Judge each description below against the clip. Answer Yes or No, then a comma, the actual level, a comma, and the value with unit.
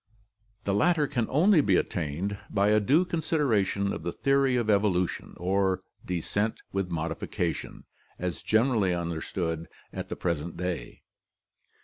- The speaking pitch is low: Yes, low, 100 Hz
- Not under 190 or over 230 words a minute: No, slow, 135 wpm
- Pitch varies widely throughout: Yes, wide, 5.7 semitones